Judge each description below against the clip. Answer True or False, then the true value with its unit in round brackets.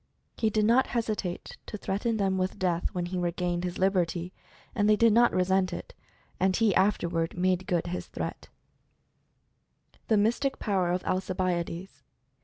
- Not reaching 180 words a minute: True (160 wpm)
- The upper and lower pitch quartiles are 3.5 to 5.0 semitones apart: False (2.9 semitones)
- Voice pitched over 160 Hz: True (185 Hz)